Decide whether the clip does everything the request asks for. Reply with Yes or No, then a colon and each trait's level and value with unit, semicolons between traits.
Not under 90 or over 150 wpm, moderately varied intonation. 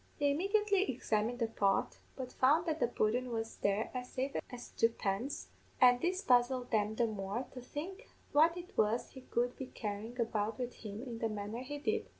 No: average, 190 wpm; average, 4.4 semitones